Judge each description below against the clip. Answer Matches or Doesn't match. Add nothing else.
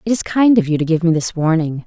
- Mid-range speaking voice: Matches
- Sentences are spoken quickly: Matches